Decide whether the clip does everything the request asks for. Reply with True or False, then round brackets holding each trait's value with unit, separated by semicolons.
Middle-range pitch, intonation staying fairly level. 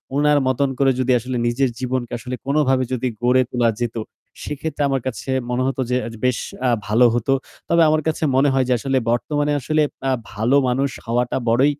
False (130 Hz; 2.3 semitones)